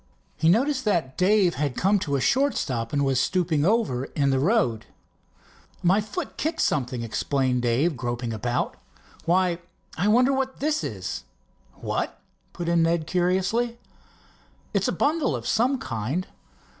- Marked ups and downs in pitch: Yes, wide, 8.8 semitones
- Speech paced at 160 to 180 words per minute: No, average, 150 wpm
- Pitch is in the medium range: Yes, medium, 170 Hz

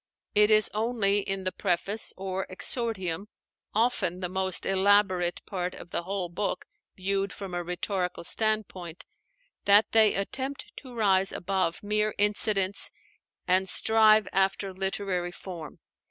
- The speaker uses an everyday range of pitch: No, narrow, 2.3 semitones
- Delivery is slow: Yes, slow, 130 wpm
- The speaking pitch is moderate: No, high, 195 Hz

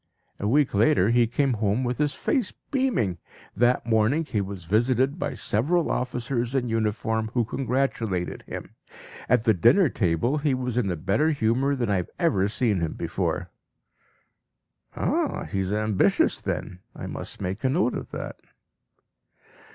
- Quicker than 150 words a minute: Yes, average, 160 wpm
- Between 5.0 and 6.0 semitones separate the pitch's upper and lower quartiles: No, average, 4.5 semitones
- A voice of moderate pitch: No, low, 120 Hz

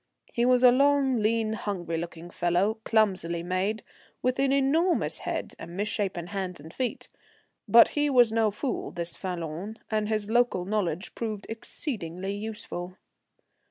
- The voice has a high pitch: Yes, high, 210 Hz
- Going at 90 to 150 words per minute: Yes, average, 145 wpm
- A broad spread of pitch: No, average, 5.0 semitones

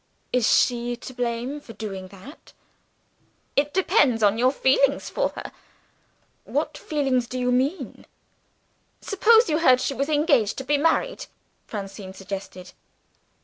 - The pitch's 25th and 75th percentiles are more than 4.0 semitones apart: Yes, average, 4.6 semitones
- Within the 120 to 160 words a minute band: Yes, slow, 135 wpm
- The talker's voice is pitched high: Yes, very high, 255 Hz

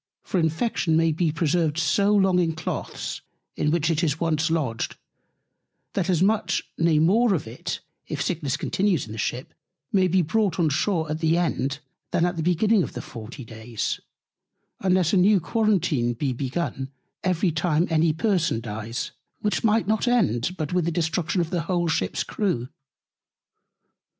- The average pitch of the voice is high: No, medium, 165 Hz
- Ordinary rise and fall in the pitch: Yes, average, 3.7 semitones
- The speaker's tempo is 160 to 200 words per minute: Yes, average, 165 wpm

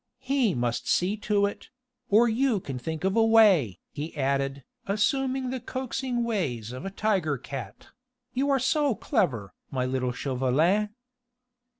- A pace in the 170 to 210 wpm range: No, average, 145 wpm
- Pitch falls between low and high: No, high, 195 Hz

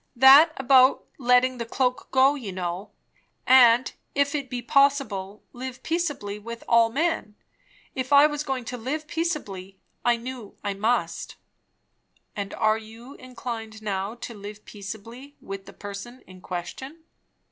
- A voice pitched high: Yes, high, 240 Hz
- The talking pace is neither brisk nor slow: Yes, average, 145 wpm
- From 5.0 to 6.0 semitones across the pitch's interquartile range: No, average, 4.3 semitones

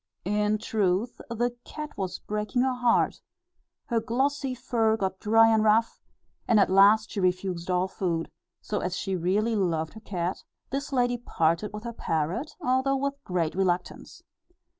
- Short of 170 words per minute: Yes, average, 160 wpm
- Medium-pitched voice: No, high, 210 Hz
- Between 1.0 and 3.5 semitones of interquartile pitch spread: No, average, 4.6 semitones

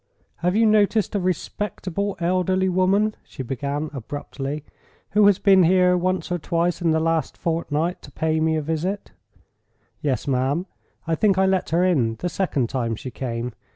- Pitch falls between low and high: Yes, medium, 170 Hz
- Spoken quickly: No, average, 170 wpm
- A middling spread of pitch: Yes, average, 4.3 semitones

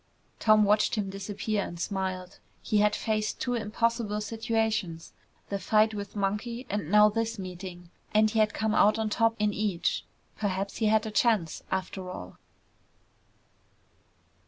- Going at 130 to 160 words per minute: Yes, average, 150 wpm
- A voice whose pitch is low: No, high, 210 Hz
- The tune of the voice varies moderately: No, narrow, 2.1 semitones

